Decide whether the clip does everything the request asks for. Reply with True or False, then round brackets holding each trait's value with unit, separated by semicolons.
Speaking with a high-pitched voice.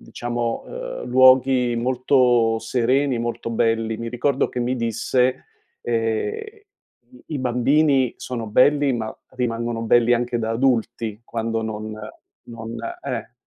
False (120 Hz)